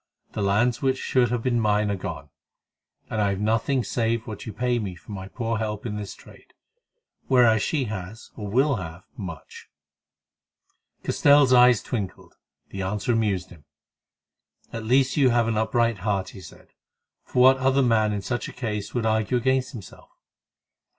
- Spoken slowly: No, average, 170 wpm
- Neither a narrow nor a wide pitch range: Yes, average, 3.3 semitones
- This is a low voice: Yes, low, 110 Hz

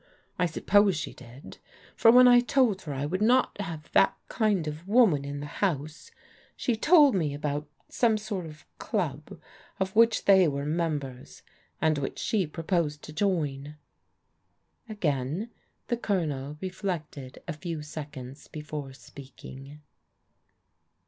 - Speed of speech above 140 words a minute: No, slow, 135 wpm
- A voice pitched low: No, medium, 160 Hz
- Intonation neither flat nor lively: No, wide, 5.7 semitones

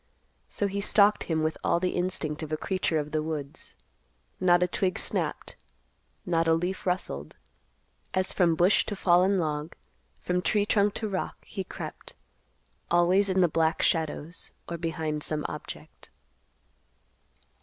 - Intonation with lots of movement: No, average, 3.0 semitones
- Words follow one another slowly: No, average, 150 wpm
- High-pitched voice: No, medium, 175 Hz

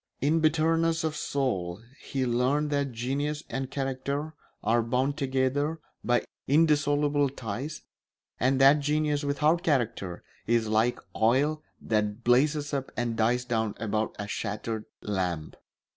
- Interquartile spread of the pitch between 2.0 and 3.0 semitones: No, average, 4.3 semitones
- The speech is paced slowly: Yes, slow, 130 wpm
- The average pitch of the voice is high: No, low, 135 Hz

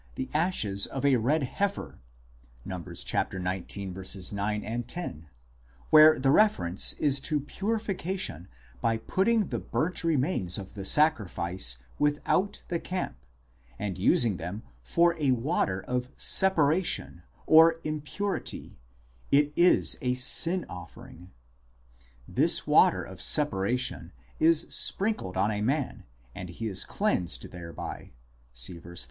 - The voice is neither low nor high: No, low, 125 Hz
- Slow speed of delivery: Yes, slow, 130 wpm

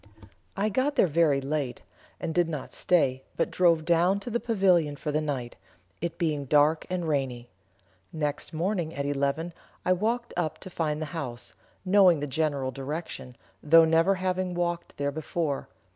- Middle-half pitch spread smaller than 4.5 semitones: Yes, average, 3.8 semitones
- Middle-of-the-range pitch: Yes, medium, 160 Hz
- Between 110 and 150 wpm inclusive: No, average, 165 wpm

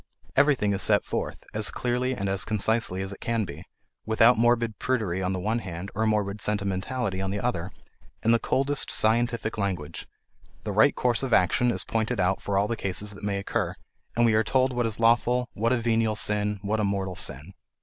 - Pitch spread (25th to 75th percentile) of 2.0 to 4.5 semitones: Yes, average, 3.1 semitones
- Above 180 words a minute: Yes, fast, 205 wpm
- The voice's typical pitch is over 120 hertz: No, low, 110 Hz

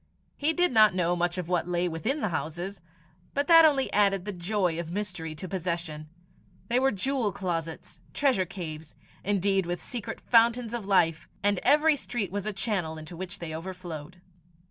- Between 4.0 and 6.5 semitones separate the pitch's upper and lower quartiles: Yes, average, 4.4 semitones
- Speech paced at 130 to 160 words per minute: No, average, 175 wpm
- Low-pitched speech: No, medium, 185 Hz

